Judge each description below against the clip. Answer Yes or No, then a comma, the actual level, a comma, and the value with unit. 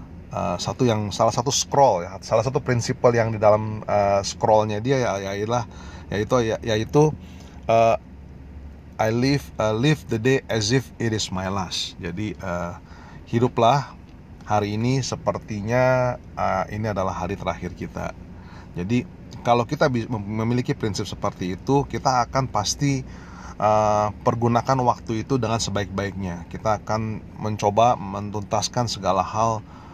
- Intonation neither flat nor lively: Yes, average, 4.6 semitones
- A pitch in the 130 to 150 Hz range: No, low, 105 Hz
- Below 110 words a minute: No, average, 130 wpm